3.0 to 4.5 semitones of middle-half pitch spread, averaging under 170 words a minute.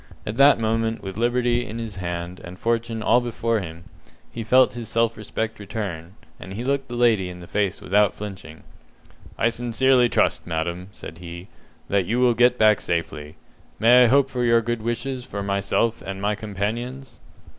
No: average, 3.8 semitones; average, 180 wpm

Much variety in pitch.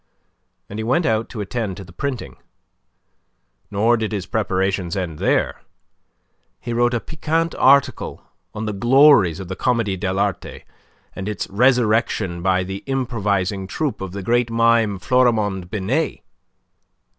No: average, 4.1 semitones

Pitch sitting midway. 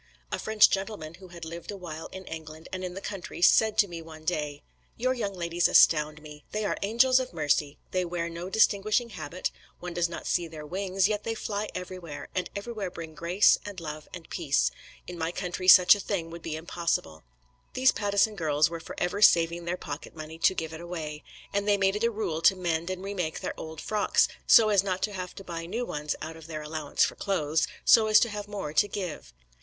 Yes: medium, 175 Hz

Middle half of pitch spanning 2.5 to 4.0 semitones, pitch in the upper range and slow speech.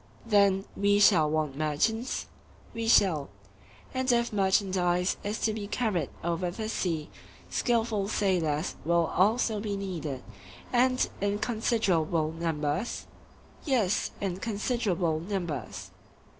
No: average, 5.0 semitones; high, 195 Hz; slow, 115 wpm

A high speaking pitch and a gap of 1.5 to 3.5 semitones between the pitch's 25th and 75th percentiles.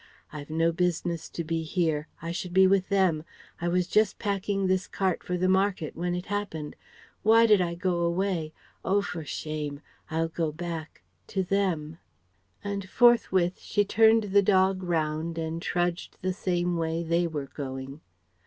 No: medium, 175 Hz; average, 2.8 semitones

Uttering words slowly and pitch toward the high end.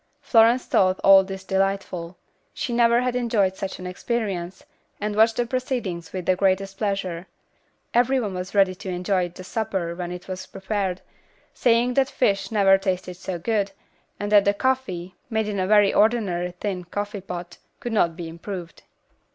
No: average, 170 wpm; high, 195 Hz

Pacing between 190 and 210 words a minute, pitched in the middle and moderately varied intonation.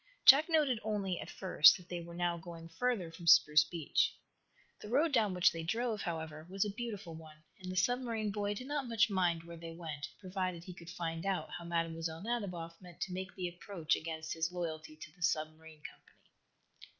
Yes: average, 200 wpm; medium, 175 Hz; average, 3.8 semitones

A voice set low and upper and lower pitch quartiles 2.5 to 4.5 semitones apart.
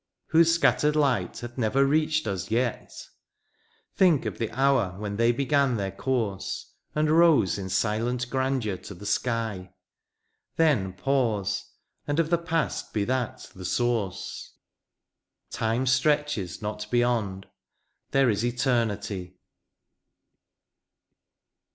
No: low, 120 Hz; average, 5.0 semitones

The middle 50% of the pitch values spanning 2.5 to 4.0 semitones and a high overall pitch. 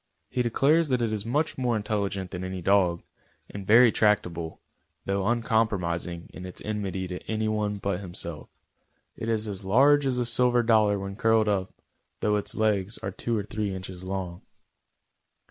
No: average, 3.3 semitones; low, 105 Hz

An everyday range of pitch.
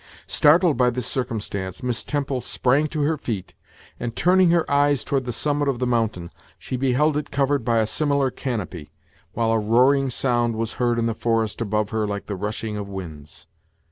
Yes: average, 4.4 semitones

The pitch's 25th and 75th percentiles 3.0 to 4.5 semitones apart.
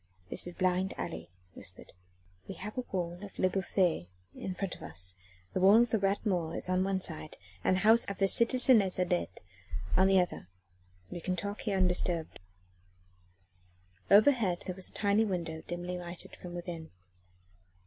No: narrow, 2.4 semitones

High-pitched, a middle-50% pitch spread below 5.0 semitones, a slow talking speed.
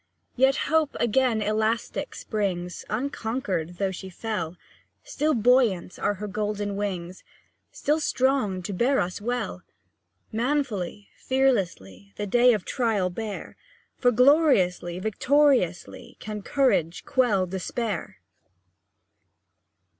No: high, 215 Hz; wide, 5.5 semitones; slow, 105 wpm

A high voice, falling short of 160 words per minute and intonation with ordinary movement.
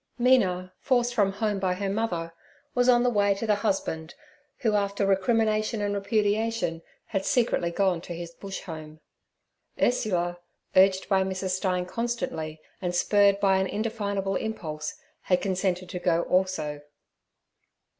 Yes: high, 195 Hz; average, 145 wpm; average, 3.0 semitones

